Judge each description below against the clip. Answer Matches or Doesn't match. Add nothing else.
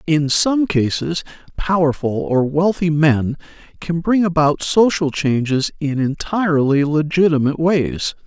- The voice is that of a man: Matches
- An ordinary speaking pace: Doesn't match